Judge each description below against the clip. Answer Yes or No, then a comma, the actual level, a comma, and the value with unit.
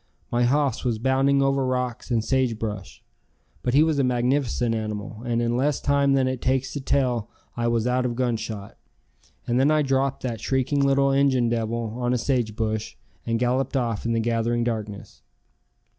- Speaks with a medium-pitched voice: No, low, 125 Hz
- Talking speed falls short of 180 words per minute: No, average, 185 wpm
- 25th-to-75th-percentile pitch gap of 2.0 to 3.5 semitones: Yes, average, 2.7 semitones